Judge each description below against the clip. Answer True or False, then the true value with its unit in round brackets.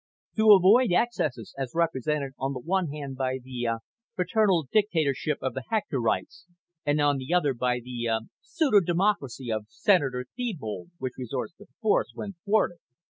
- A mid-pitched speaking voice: True (145 Hz)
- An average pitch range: False (7.0 semitones)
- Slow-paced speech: False (160 wpm)